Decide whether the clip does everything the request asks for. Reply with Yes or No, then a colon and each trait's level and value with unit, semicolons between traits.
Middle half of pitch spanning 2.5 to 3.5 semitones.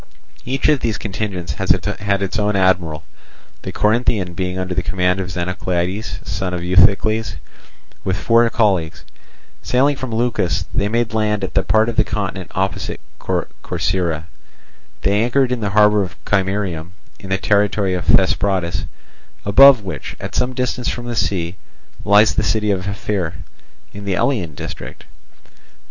Yes: average, 3.1 semitones